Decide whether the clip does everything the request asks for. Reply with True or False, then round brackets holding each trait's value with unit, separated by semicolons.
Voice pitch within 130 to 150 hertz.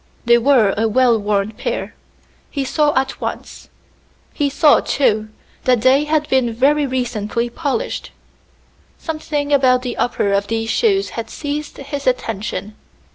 False (255 Hz)